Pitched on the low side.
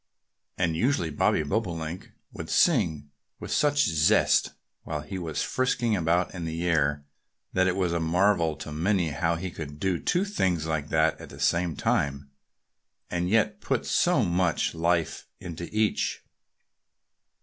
Yes: very low, 85 Hz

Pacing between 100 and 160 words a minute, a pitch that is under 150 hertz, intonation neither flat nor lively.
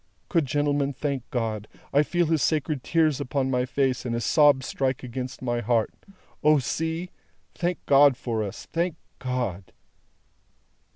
Yes: average, 150 wpm; low, 135 Hz; average, 3.5 semitones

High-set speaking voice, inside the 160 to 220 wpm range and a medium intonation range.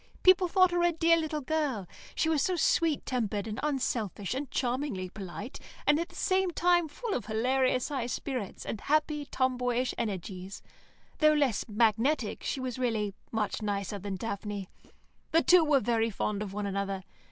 No: very high, 250 Hz; average, 170 wpm; wide, 6.6 semitones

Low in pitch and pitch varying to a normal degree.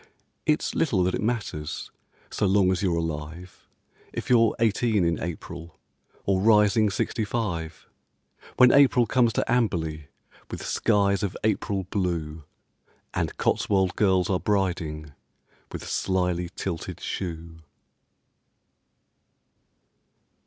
Yes: very low, 95 Hz; average, 4.2 semitones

